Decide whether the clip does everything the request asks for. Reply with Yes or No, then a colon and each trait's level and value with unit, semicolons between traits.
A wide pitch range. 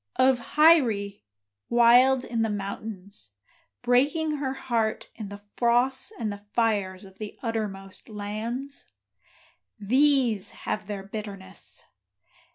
No: average, 4.2 semitones